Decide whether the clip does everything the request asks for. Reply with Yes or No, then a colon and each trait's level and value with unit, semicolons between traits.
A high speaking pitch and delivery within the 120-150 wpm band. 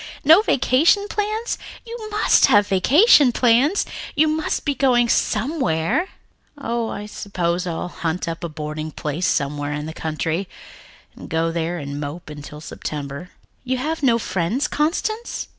Yes: high, 195 Hz; average, 145 wpm